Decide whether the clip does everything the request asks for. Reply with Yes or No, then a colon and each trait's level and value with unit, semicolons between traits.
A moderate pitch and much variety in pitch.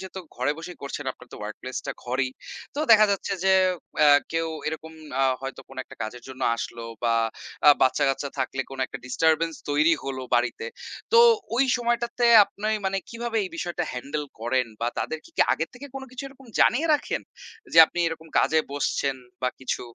Yes: medium, 155 Hz; wide, 7.2 semitones